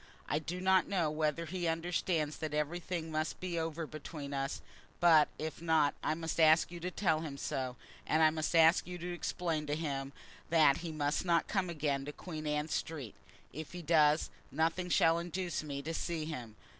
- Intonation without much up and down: Yes, narrow, 2.2 semitones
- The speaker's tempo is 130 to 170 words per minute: No, average, 195 wpm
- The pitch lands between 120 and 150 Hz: No, medium, 160 Hz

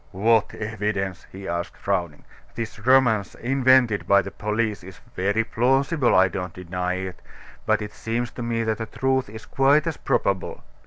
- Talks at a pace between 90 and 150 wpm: No, average, 165 wpm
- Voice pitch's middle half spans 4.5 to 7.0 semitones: No, average, 4.0 semitones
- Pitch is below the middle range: Yes, low, 110 Hz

